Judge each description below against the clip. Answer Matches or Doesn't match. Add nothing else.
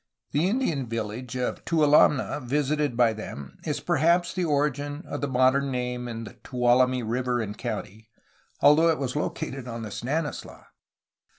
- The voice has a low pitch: Matches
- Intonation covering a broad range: Doesn't match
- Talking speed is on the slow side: Doesn't match